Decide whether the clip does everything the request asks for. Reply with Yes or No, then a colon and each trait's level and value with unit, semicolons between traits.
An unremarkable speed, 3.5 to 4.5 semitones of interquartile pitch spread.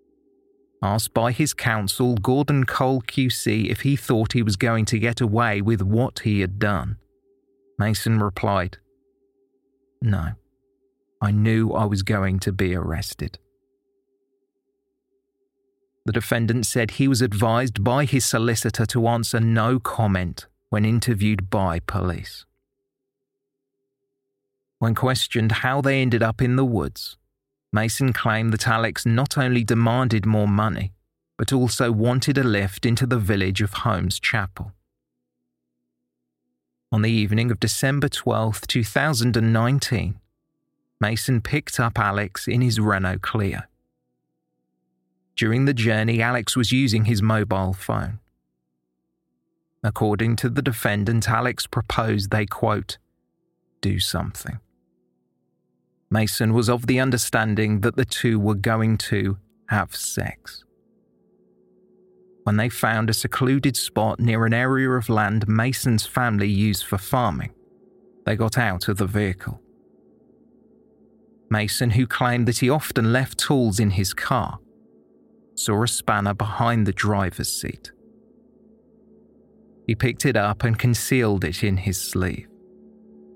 No: slow, 125 wpm; average, 4.1 semitones